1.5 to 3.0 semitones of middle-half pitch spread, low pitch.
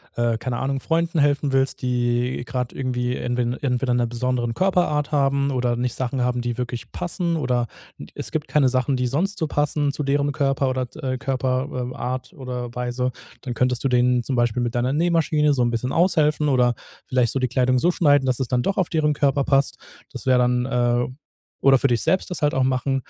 Yes: narrow, 2.6 semitones; low, 130 Hz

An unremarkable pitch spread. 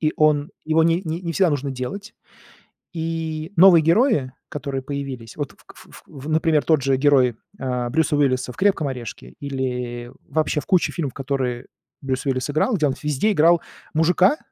Yes: average, 3.8 semitones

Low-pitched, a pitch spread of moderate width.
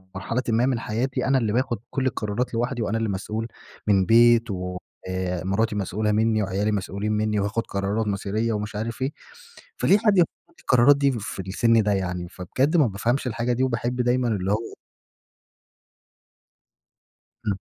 Yes: low, 110 Hz; average, 3.3 semitones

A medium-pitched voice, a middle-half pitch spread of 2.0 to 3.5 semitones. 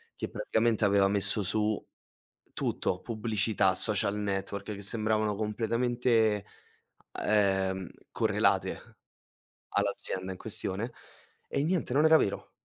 No: low, 105 Hz; narrow, 2.6 semitones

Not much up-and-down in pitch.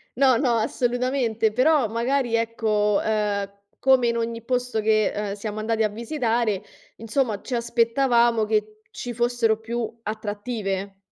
Yes: narrow, 2.1 semitones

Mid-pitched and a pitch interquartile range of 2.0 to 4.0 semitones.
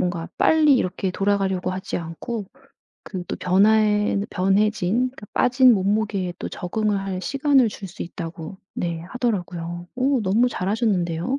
No: high, 195 Hz; average, 3.5 semitones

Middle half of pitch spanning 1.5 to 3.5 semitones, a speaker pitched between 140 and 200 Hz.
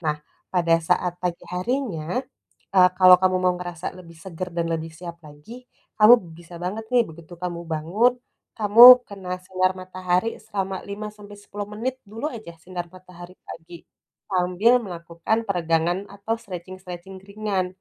Yes: average, 3.2 semitones; medium, 185 Hz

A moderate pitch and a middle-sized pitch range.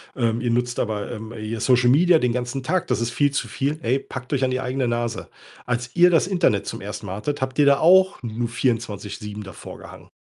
No: low, 125 Hz; average, 3.3 semitones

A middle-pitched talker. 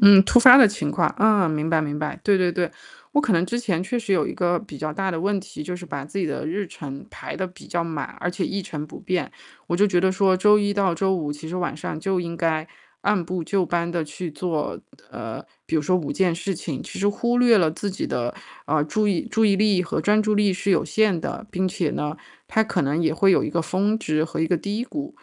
Yes: medium, 180 Hz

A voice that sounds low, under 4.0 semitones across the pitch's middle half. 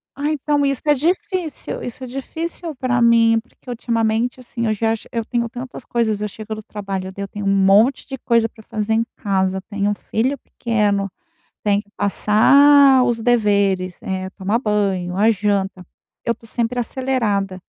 No: high, 225 Hz; average, 3.6 semitones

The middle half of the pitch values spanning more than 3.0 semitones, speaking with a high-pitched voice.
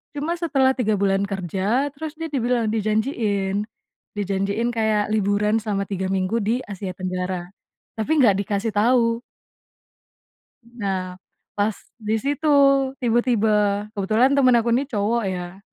Yes: average, 3.4 semitones; high, 215 Hz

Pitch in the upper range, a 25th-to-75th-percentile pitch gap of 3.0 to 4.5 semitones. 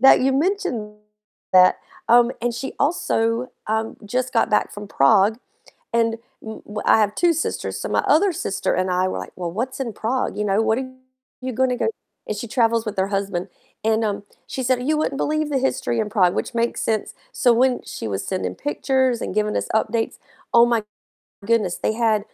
Yes: high, 230 Hz; average, 3.6 semitones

